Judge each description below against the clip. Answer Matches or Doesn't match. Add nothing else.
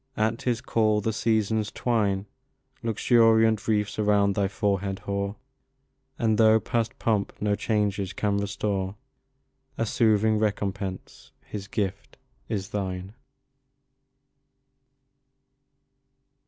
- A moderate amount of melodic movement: Doesn't match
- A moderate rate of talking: Doesn't match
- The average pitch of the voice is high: Doesn't match